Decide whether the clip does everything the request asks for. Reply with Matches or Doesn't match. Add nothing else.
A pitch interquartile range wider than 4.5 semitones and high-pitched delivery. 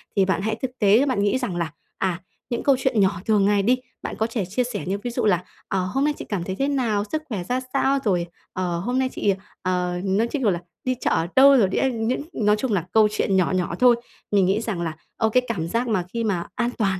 Matches